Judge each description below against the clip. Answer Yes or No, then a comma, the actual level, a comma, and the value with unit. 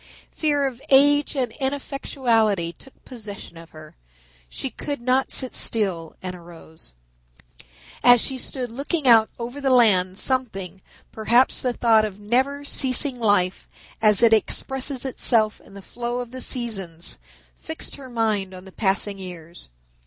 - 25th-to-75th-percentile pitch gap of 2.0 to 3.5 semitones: No, average, 5.2 semitones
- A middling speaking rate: Yes, average, 145 wpm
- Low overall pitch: No, high, 235 Hz